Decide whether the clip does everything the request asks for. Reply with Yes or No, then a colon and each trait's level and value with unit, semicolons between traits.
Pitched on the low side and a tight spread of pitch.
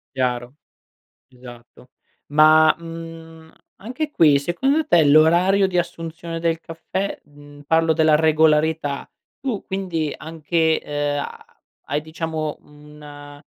No: medium, 160 Hz; narrow, 2.2 semitones